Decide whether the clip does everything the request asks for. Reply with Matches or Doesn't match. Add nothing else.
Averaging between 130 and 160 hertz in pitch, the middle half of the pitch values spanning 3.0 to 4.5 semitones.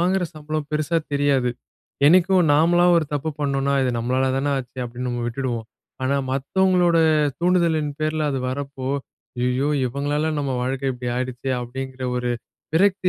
Matches